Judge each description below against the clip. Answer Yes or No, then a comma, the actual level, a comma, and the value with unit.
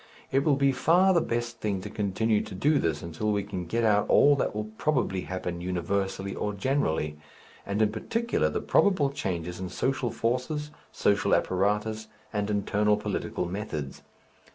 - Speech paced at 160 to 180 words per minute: Yes, average, 165 wpm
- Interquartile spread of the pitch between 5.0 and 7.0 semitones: Yes, wide, 5.6 semitones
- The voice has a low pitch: Yes, low, 105 Hz